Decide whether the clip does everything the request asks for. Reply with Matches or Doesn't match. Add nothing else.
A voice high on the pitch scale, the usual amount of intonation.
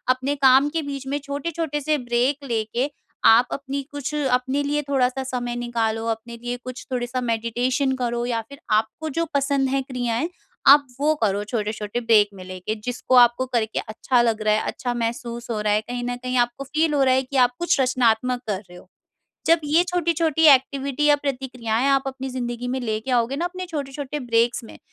Matches